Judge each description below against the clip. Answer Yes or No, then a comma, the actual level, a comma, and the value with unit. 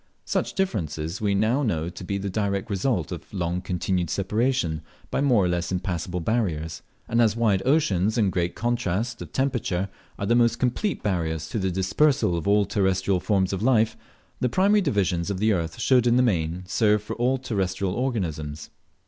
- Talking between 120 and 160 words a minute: No, average, 180 wpm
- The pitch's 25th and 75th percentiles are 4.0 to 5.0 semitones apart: Yes, average, 4.7 semitones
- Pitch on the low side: Yes, low, 100 Hz